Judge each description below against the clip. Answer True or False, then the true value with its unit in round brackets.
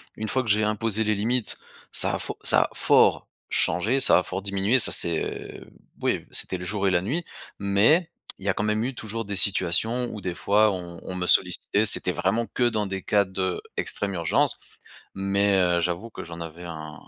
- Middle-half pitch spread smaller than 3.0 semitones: False (3.3 semitones)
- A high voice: False (100 Hz)